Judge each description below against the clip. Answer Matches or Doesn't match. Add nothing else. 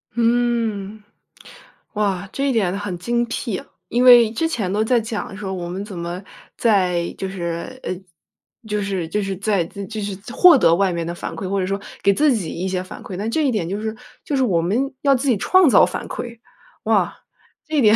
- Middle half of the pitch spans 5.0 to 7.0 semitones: Doesn't match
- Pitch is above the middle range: Matches